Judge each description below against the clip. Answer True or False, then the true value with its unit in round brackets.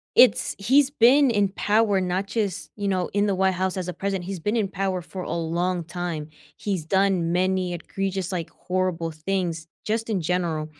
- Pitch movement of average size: False (2.3 semitones)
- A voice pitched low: False (185 Hz)